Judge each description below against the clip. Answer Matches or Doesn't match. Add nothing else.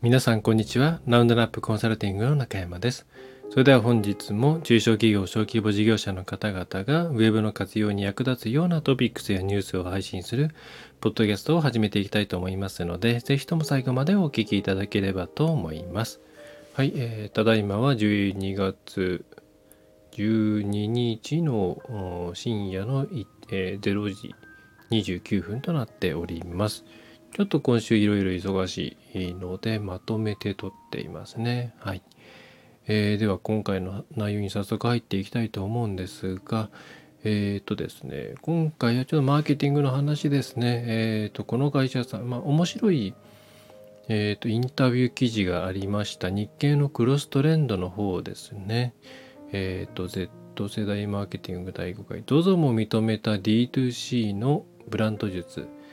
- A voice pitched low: Matches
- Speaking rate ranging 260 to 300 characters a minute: Doesn't match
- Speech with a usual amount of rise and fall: Matches